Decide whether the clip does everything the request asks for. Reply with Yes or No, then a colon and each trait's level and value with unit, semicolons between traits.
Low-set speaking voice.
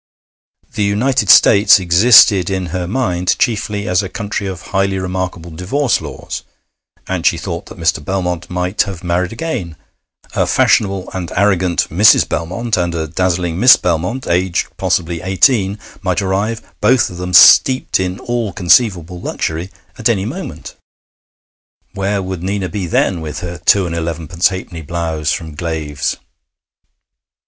Yes: very low, 90 Hz